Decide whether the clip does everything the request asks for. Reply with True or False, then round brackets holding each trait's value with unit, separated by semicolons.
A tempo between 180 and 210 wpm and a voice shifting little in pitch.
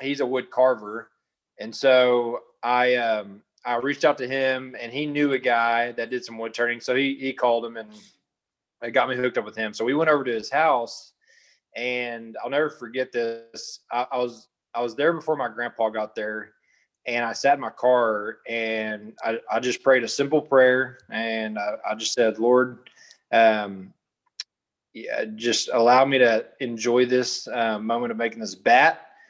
True (190 wpm; 2.2 semitones)